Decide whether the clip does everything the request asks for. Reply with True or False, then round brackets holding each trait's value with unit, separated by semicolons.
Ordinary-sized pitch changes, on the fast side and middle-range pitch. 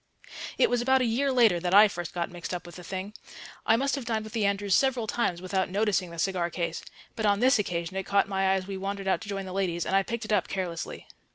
False (3.3 semitones; 270 wpm; 195 Hz)